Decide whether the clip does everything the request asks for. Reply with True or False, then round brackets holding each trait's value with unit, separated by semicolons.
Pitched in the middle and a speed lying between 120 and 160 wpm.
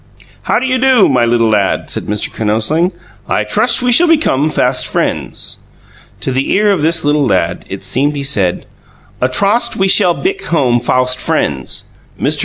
False (145 Hz; 180 wpm)